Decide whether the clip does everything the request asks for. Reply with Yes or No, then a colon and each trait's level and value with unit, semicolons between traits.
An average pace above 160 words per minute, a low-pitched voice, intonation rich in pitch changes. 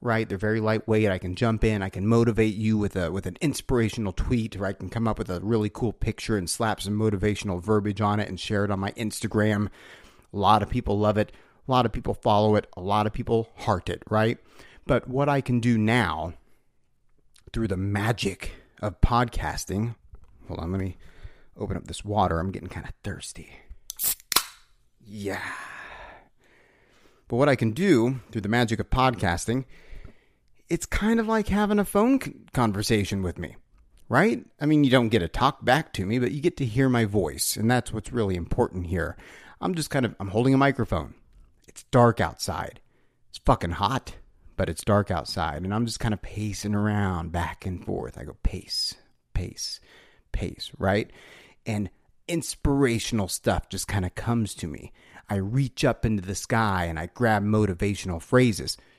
No: average, 185 wpm; low, 105 Hz; average, 3.7 semitones